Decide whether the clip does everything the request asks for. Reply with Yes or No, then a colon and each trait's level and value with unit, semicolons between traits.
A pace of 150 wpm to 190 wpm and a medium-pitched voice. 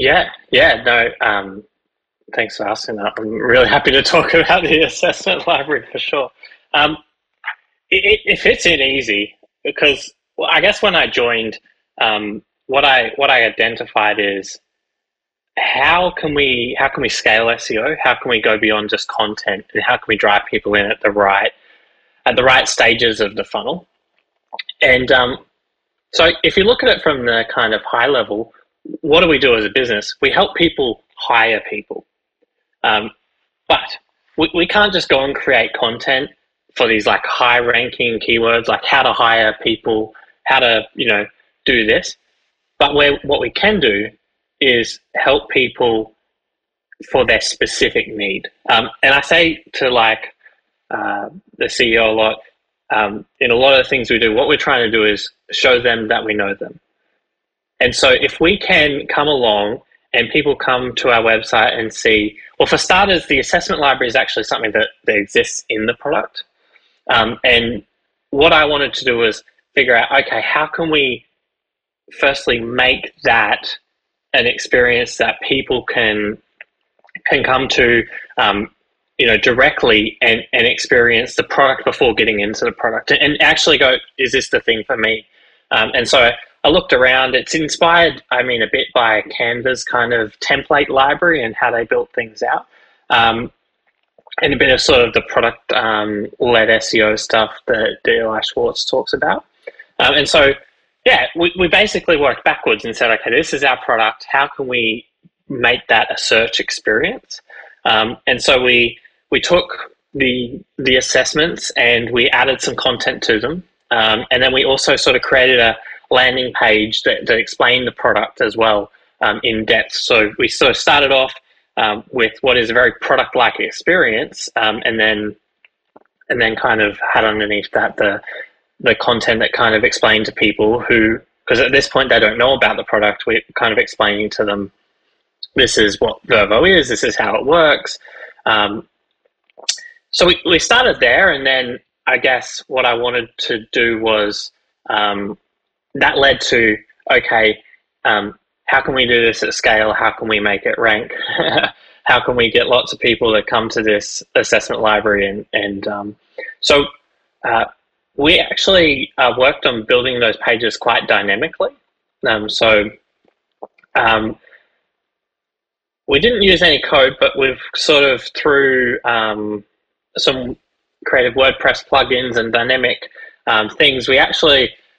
No: average, 170 wpm; low, 125 Hz